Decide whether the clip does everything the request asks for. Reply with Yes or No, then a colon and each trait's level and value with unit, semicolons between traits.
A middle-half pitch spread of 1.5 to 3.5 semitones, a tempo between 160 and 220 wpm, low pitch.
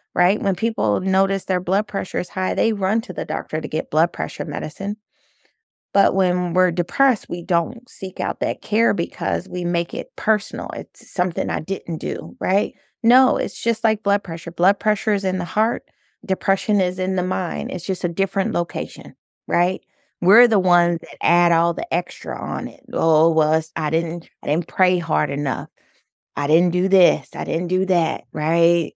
No: average, 3.1 semitones; average, 190 wpm; medium, 185 Hz